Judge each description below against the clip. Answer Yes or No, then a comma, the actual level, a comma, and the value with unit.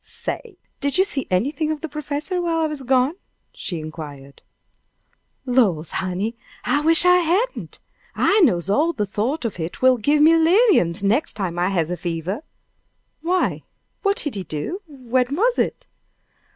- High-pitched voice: Yes, very high, 260 Hz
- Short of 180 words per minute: Yes, average, 165 wpm